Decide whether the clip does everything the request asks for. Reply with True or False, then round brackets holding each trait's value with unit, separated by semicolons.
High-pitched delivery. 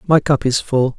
False (140 Hz)